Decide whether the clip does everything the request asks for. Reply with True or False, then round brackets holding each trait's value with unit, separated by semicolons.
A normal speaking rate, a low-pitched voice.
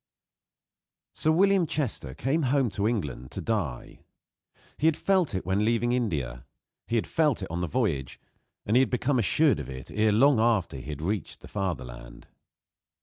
True (175 wpm; 110 Hz)